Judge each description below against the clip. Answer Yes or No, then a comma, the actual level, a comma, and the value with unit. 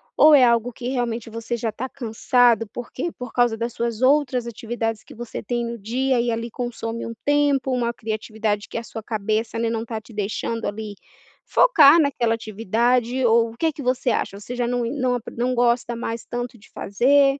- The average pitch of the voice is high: Yes, high, 235 Hz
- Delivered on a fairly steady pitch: Yes, narrow, 1.8 semitones